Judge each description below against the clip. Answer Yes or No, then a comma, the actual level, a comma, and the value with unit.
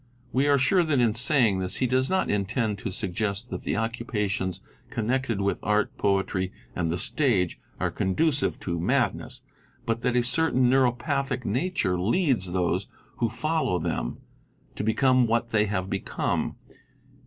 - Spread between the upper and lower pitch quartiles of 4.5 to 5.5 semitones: Yes, average, 5.0 semitones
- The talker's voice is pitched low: Yes, low, 115 Hz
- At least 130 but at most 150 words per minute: No, average, 160 wpm